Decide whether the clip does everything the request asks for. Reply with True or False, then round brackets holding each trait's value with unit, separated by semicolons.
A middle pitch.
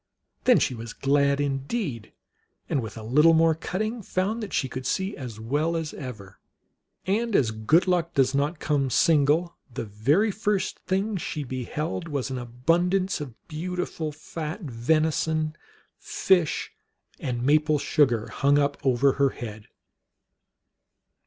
True (150 Hz)